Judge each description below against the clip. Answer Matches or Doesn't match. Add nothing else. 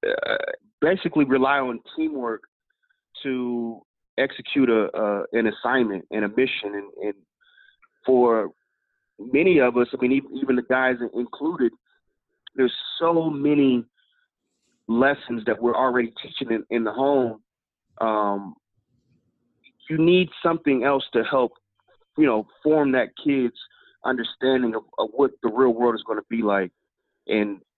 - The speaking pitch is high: Doesn't match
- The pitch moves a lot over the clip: Matches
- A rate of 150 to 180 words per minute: Doesn't match